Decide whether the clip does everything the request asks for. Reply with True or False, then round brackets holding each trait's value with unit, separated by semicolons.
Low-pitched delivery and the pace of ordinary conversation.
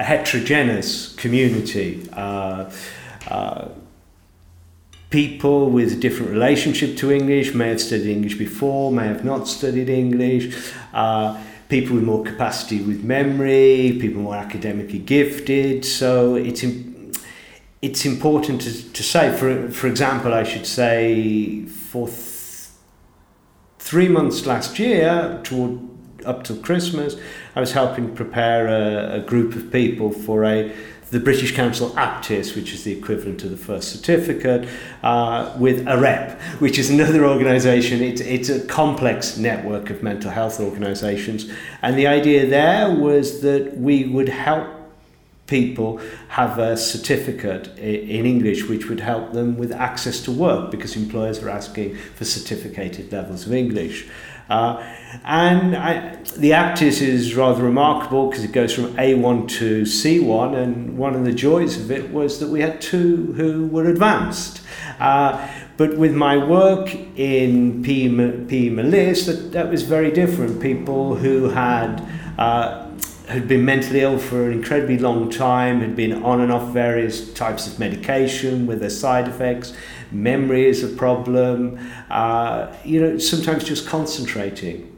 True (125 Hz; 145 wpm)